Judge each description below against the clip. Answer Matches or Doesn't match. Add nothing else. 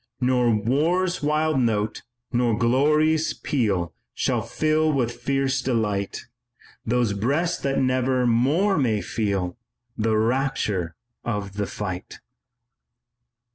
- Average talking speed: Doesn't match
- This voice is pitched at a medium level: Doesn't match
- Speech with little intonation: Doesn't match